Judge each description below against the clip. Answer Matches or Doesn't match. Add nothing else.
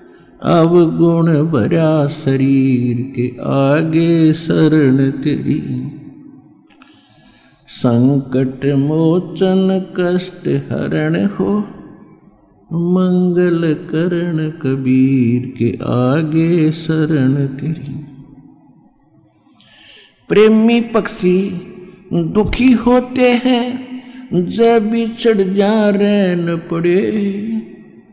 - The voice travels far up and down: Matches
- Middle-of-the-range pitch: Matches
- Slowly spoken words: Matches